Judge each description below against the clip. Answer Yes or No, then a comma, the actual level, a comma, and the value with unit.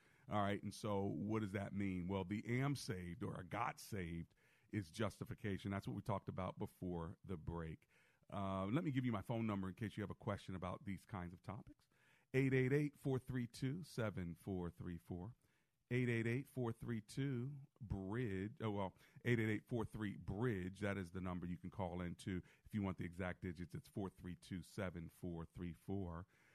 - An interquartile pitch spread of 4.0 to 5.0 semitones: Yes, average, 4.7 semitones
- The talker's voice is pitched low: Yes, low, 100 Hz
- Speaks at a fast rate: No, average, 165 wpm